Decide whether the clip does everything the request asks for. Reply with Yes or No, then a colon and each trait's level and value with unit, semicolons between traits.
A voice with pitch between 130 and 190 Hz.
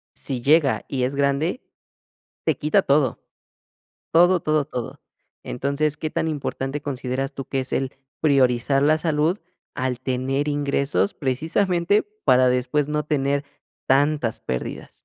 Yes: medium, 140 Hz